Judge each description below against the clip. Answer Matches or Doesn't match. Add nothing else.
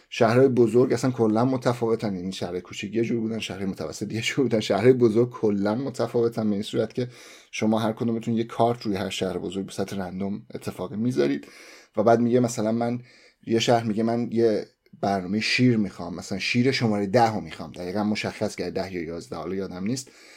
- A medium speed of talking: Doesn't match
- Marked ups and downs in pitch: Doesn't match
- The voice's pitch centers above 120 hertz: Doesn't match